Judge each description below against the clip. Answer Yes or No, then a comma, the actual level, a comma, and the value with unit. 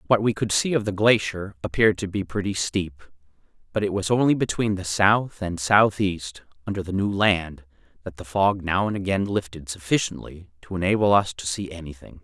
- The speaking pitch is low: Yes, very low, 95 Hz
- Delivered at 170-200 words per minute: Yes, average, 190 wpm